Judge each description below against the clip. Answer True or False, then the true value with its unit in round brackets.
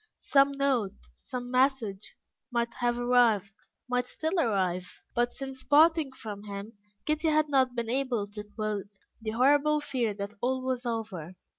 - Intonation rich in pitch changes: False (4.3 semitones)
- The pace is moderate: True (150 wpm)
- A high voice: True (245 Hz)